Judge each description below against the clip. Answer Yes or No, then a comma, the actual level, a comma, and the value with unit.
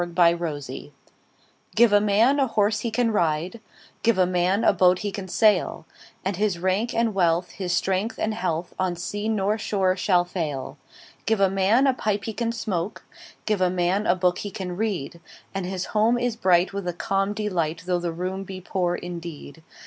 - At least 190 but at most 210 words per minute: Yes, average, 195 wpm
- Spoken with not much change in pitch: No, average, 3.3 semitones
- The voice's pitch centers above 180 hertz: Yes, high, 190 Hz